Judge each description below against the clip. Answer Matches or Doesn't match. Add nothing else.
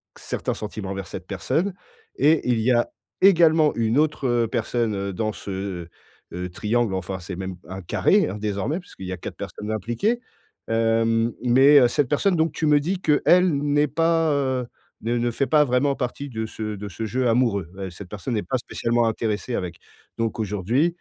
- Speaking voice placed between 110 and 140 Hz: Matches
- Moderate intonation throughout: Doesn't match